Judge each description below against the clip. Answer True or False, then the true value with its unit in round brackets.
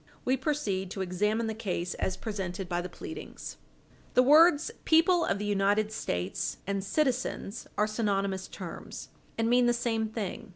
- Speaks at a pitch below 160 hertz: False (215 Hz)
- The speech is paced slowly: False (160 wpm)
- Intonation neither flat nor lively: True (4.3 semitones)